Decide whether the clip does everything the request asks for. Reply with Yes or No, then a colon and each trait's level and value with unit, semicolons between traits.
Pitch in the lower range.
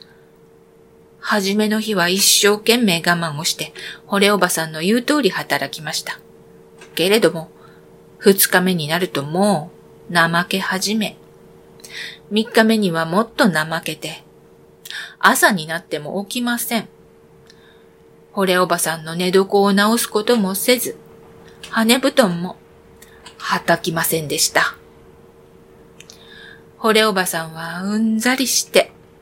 No: medium, 170 Hz